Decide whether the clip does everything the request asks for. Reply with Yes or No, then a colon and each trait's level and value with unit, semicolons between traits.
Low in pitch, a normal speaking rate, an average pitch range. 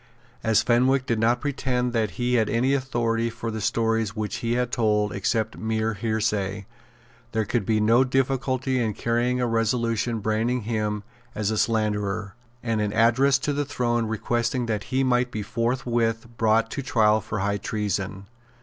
No: low, 115 Hz; average, 170 wpm; narrow, 2.3 semitones